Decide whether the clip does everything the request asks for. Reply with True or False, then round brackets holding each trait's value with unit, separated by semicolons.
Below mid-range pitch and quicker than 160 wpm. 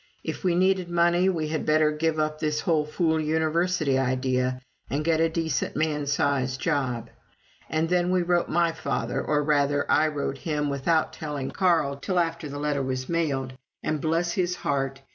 False (155 Hz; 180 wpm)